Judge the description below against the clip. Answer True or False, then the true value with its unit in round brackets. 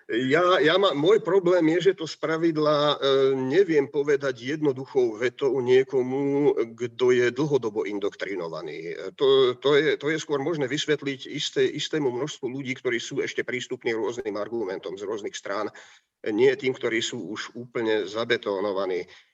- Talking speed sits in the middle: True (150 wpm)